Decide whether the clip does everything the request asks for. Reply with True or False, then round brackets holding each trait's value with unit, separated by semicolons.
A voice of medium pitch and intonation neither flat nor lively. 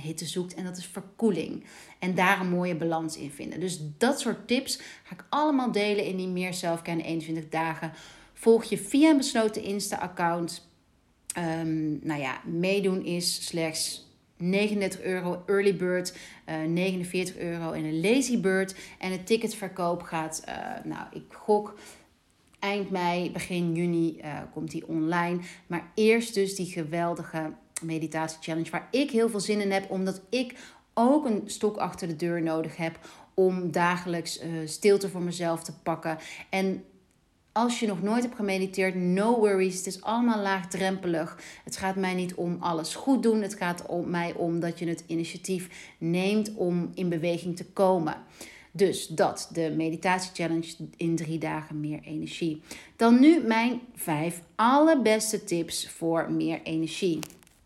True (180 Hz; 3.4 semitones)